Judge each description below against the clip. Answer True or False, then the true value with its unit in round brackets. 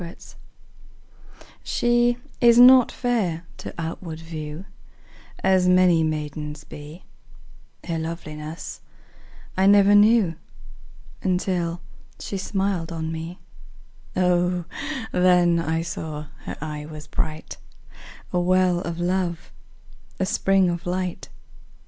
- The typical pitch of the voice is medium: True (175 Hz)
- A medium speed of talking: False (105 wpm)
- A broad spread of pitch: False (2.7 semitones)